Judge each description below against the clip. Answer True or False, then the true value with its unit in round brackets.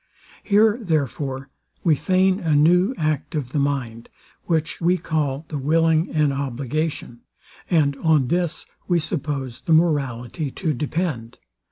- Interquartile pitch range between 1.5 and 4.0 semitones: True (3.5 semitones)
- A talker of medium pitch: True (155 Hz)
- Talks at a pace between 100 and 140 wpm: True (135 wpm)